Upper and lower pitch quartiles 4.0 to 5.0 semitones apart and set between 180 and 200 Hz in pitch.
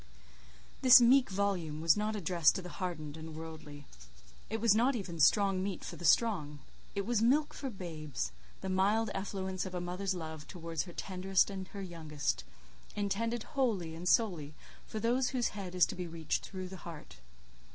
Yes: average, 4.4 semitones; medium, 185 Hz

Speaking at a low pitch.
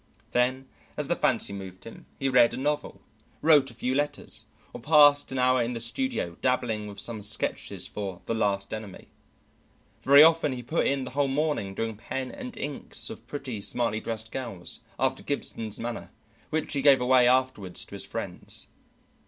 Yes: low, 125 Hz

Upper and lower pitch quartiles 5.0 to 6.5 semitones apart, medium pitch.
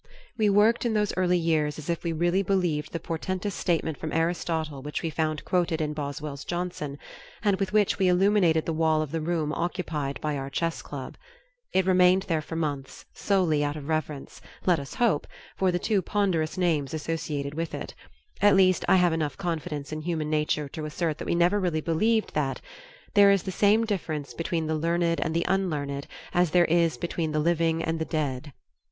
No: average, 3.0 semitones; medium, 165 Hz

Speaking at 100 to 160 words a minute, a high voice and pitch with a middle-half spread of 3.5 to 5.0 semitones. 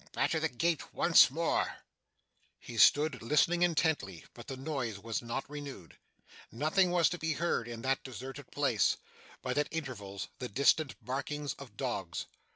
No: average, 155 wpm; low, 135 Hz; average, 4.7 semitones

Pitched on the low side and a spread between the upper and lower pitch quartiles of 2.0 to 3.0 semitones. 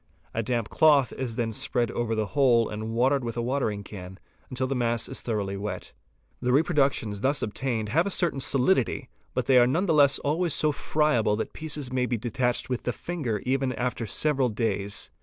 No: low, 125 Hz; average, 3.8 semitones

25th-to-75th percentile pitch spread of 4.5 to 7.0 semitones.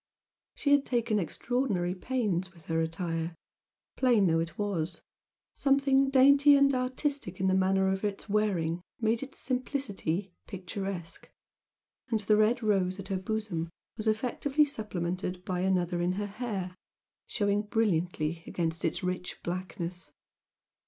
Yes: average, 4.8 semitones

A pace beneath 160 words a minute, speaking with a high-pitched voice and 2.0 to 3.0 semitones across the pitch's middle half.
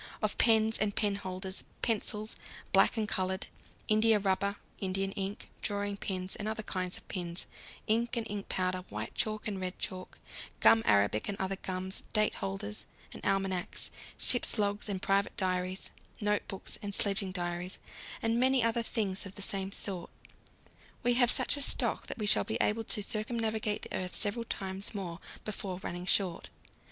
No: average, 165 wpm; high, 200 Hz; narrow, 2.5 semitones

